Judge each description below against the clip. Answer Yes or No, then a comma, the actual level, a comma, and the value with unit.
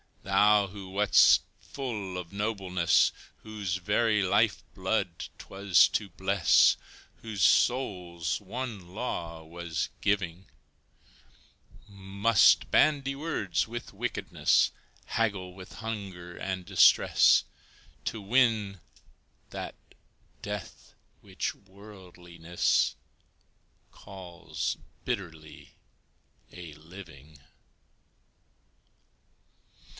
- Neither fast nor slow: No, slow, 80 wpm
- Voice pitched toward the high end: No, very low, 95 Hz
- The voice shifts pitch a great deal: No, average, 3.2 semitones